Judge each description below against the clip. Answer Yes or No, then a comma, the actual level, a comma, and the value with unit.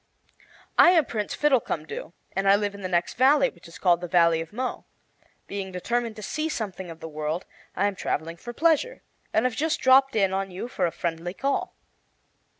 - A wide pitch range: Yes, wide, 6.7 semitones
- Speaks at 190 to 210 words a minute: Yes, average, 200 wpm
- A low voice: No, high, 200 Hz